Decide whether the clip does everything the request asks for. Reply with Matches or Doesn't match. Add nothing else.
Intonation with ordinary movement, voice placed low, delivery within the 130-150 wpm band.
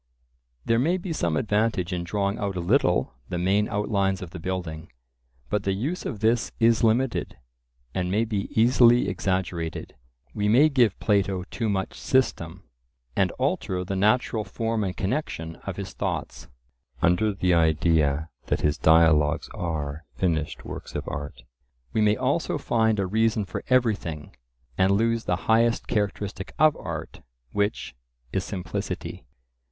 Matches